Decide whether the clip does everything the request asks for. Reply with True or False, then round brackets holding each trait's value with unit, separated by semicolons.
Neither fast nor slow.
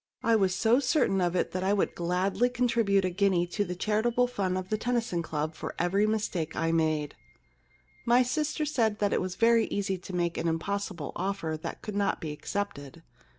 False (210 wpm)